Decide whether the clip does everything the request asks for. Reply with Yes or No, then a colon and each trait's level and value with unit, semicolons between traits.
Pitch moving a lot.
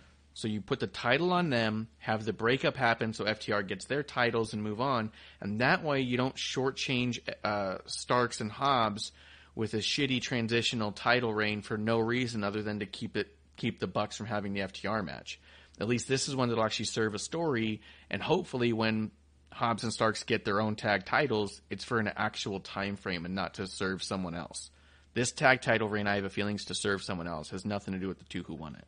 No: average, 3.4 semitones